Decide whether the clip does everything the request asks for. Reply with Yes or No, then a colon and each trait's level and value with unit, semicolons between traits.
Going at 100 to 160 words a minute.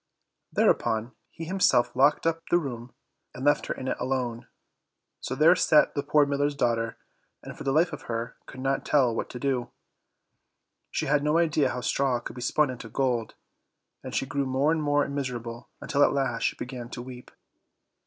No: average, 190 wpm